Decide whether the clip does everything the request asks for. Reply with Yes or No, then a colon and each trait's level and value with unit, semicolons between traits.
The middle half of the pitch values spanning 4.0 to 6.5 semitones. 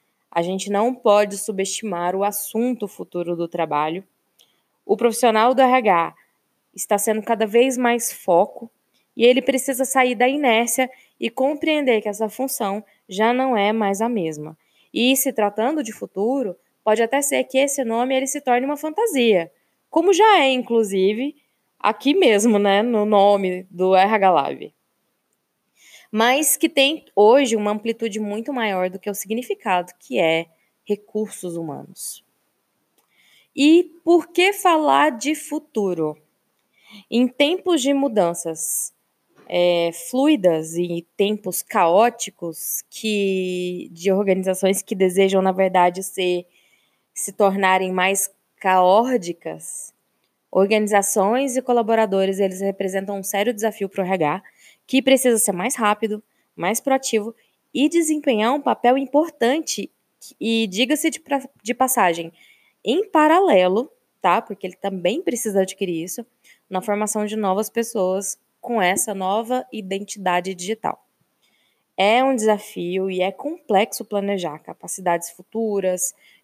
Yes: average, 5.0 semitones